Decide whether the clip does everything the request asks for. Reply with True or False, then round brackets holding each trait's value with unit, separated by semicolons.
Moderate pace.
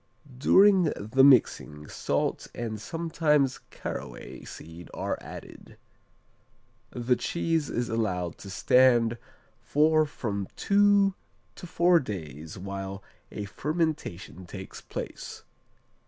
False (100 wpm)